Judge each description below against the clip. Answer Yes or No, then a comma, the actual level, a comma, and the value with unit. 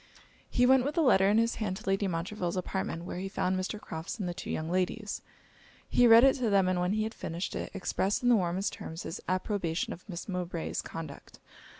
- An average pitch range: Yes, average, 3.5 semitones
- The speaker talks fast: Yes, fast, 225 wpm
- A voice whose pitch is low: No, high, 190 Hz